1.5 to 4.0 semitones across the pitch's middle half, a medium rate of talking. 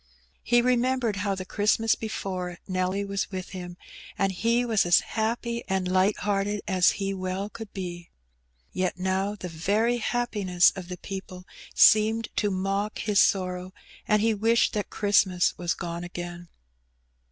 Yes: average, 2.9 semitones; average, 150 wpm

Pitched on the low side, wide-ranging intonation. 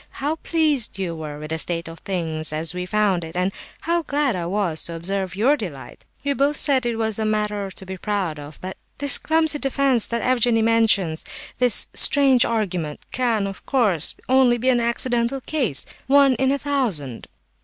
No: high, 220 Hz; wide, 6.8 semitones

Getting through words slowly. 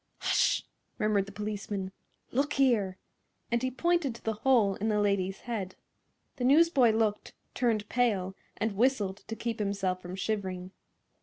No: average, 150 wpm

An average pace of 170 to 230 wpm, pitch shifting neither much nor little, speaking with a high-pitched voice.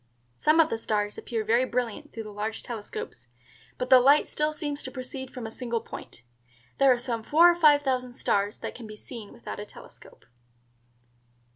Yes: average, 190 wpm; average, 3.9 semitones; high, 245 Hz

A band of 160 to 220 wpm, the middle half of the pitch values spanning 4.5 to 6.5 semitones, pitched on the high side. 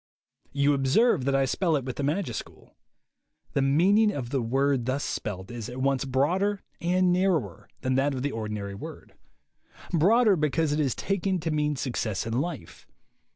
No: average, 170 wpm; average, 5.2 semitones; medium, 140 Hz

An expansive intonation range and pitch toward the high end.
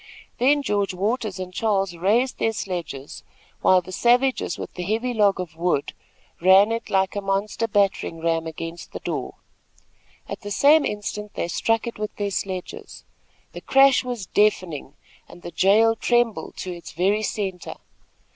No: average, 3.8 semitones; high, 200 Hz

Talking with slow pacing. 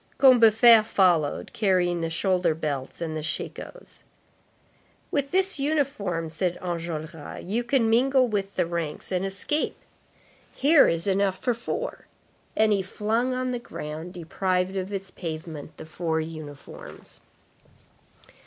Yes: slow, 130 wpm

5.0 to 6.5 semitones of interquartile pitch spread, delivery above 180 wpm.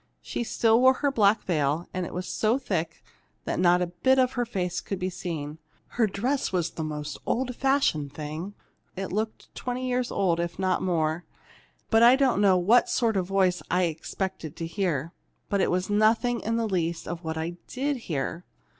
Yes: wide, 5.4 semitones; average, 200 wpm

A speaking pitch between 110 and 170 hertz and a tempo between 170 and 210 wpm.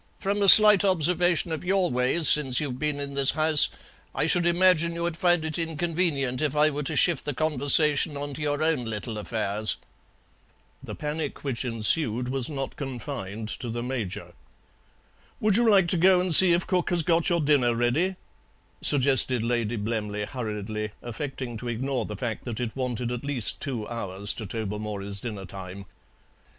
Yes: low, 135 Hz; average, 175 wpm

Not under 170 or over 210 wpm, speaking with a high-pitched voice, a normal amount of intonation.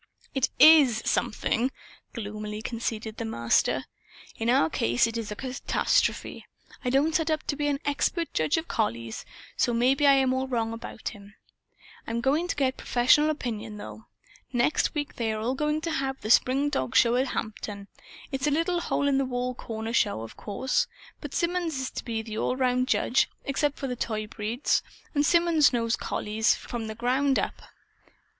Yes: average, 180 wpm; very high, 250 Hz; average, 4.3 semitones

